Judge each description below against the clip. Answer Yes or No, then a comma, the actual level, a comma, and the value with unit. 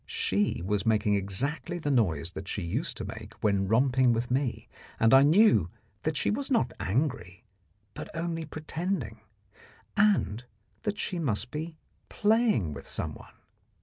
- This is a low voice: Yes, low, 125 Hz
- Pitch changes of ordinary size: No, wide, 8.1 semitones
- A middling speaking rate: Yes, average, 150 wpm